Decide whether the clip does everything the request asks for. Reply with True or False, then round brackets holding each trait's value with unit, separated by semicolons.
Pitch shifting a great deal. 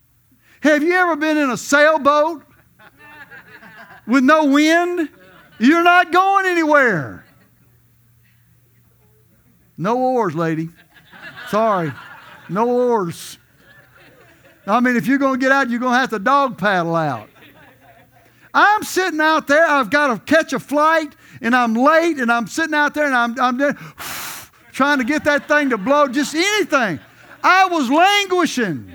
True (7.1 semitones)